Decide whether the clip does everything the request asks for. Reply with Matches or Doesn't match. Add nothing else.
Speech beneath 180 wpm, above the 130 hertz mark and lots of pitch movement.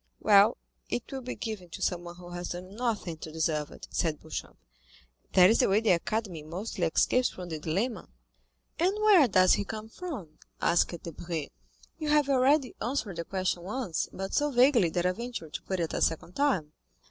Doesn't match